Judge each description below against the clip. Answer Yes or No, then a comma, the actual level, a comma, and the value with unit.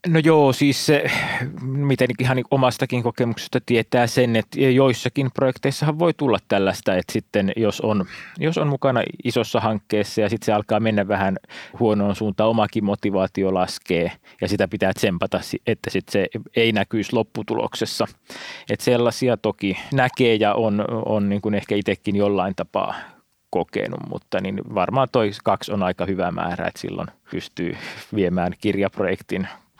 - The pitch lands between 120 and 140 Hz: No, low, 110 Hz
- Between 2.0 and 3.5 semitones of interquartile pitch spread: No, average, 3.9 semitones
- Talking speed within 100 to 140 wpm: No, average, 150 wpm